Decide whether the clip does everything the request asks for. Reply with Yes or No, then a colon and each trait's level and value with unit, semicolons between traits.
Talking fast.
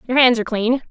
Yes: fast, 265 wpm